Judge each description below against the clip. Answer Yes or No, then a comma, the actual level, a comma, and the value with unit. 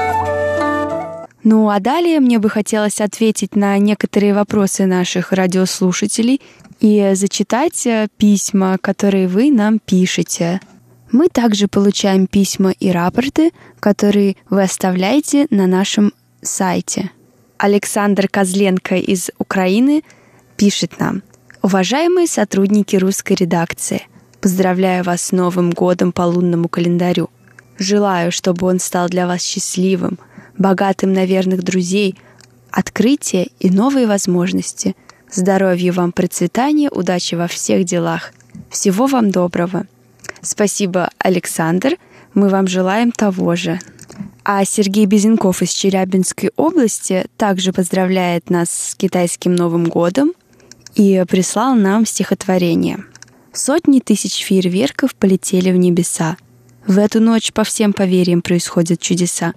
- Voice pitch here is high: Yes, high, 195 Hz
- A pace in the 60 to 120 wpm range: Yes, slow, 110 wpm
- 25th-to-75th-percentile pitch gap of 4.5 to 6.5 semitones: No, narrow, 2.6 semitones